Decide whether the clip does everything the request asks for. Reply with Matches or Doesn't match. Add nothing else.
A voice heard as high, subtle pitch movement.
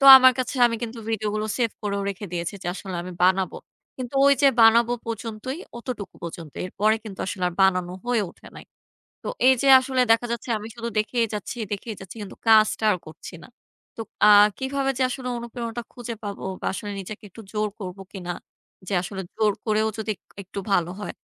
Doesn't match